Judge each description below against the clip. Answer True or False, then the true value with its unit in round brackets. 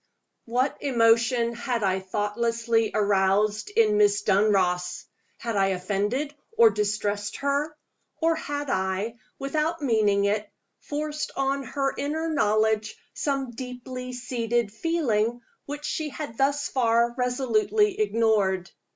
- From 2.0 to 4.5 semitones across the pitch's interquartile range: False (4.9 semitones)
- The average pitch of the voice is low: False (235 Hz)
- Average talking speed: False (115 wpm)